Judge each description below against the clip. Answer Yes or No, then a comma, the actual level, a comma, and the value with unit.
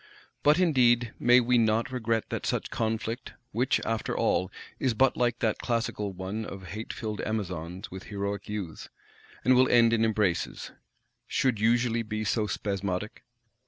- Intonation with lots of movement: No, average, 3.0 semitones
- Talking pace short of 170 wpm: Yes, average, 145 wpm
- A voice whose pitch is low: Yes, low, 110 Hz